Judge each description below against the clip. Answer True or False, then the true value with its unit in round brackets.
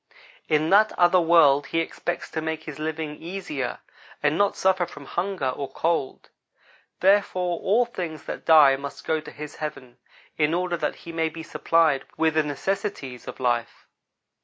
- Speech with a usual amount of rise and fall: True (3.1 semitones)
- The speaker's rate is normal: True (165 wpm)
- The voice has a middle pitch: True (160 Hz)